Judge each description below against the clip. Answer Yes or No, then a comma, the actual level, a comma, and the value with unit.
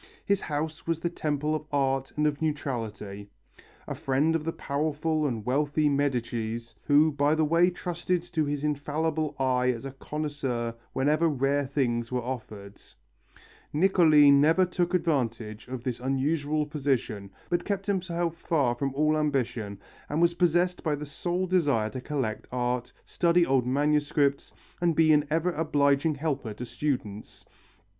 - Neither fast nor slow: Yes, average, 150 wpm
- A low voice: No, medium, 145 Hz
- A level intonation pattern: No, average, 3.7 semitones